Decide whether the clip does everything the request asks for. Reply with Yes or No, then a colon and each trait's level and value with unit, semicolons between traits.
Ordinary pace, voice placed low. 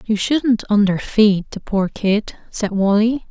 No: average, 145 wpm; high, 210 Hz